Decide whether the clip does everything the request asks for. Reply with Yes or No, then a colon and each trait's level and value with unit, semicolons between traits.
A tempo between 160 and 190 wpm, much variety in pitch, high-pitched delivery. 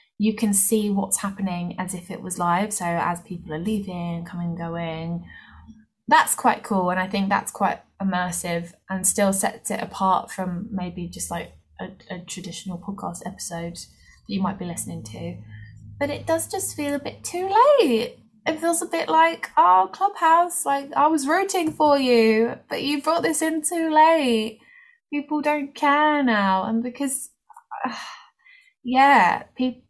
Yes: average, 170 wpm; wide, 8.7 semitones; high, 215 Hz